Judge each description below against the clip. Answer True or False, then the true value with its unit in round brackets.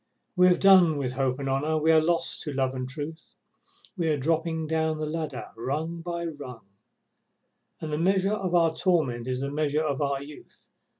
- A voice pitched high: False (155 Hz)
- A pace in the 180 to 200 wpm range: True (190 wpm)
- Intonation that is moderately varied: True (3.2 semitones)